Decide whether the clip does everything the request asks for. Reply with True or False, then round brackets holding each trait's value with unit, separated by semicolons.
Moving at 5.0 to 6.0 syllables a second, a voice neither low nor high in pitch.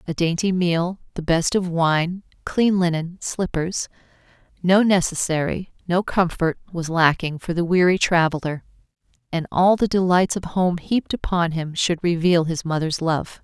False (4.5 syllables/s; 175 Hz)